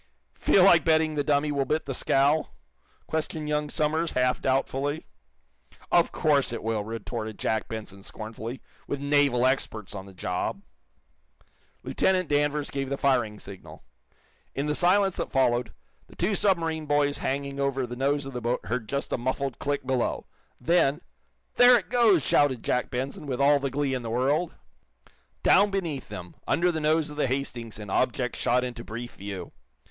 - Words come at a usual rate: Yes, average, 170 wpm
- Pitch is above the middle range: No, medium, 140 Hz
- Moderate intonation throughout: Yes, average, 3.8 semitones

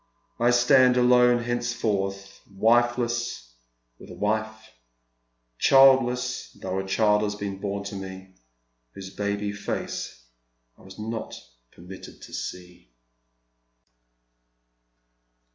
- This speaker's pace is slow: Yes, slow, 100 wpm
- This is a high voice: No, low, 105 Hz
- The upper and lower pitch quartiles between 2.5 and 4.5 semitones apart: Yes, average, 3.8 semitones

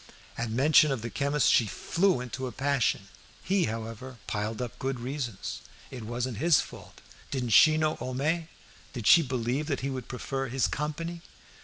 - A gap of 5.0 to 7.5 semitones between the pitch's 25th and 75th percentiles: No, average, 3.9 semitones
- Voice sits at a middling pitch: No, low, 130 Hz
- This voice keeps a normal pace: Yes, average, 170 wpm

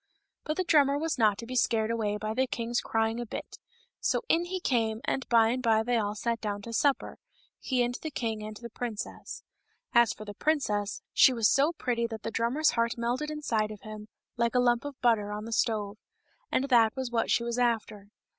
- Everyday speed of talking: No, fast, 225 wpm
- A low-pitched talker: No, high, 235 Hz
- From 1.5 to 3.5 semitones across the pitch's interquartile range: Yes, average, 2.8 semitones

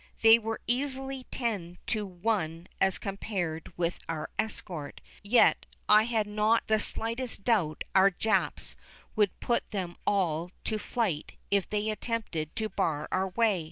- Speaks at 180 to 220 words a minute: No, average, 145 wpm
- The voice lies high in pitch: Yes, high, 205 Hz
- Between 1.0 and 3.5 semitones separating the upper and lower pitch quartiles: No, average, 4.2 semitones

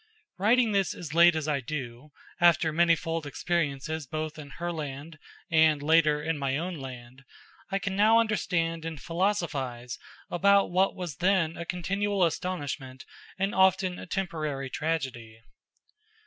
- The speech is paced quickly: No, slow, 135 wpm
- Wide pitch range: No, average, 4.1 semitones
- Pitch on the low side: No, medium, 165 Hz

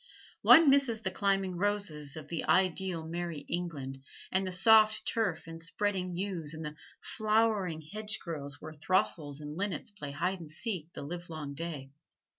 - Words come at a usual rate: Yes, average, 155 wpm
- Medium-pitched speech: Yes, medium, 175 Hz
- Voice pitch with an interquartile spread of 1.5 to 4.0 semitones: No, average, 4.5 semitones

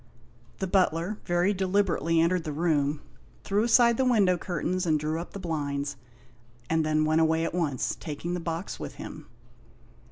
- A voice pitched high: No, medium, 170 Hz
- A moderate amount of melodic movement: Yes, average, 3.1 semitones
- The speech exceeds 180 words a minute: No, average, 165 wpm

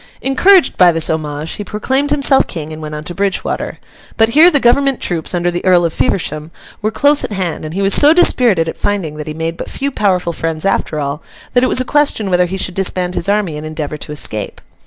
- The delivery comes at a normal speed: No, fast, 235 wpm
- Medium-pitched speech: Yes, medium, 180 Hz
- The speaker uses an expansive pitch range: Yes, wide, 7.0 semitones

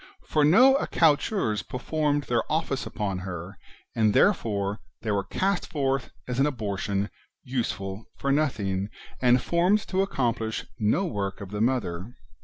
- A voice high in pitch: No, low, 120 Hz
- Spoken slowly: No, average, 145 wpm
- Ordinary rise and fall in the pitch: No, wide, 6.8 semitones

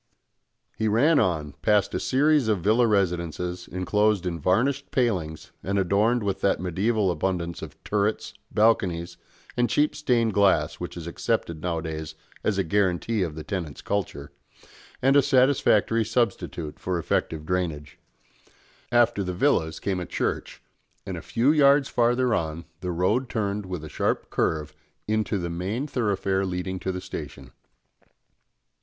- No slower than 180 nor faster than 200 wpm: No, average, 150 wpm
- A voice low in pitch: Yes, very low, 95 Hz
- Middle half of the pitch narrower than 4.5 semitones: No, average, 5.0 semitones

